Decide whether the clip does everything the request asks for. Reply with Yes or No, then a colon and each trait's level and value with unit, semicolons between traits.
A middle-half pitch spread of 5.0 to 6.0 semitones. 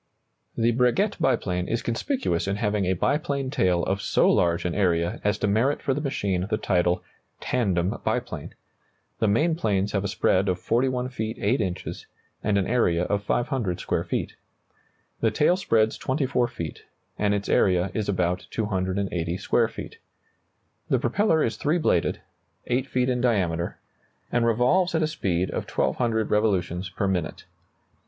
Yes: average, 5.3 semitones